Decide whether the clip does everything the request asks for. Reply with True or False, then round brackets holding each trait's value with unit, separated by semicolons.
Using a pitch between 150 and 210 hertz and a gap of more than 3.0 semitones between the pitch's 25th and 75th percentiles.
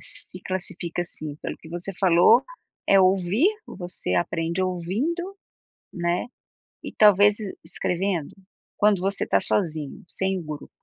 False (185 Hz; 2.7 semitones)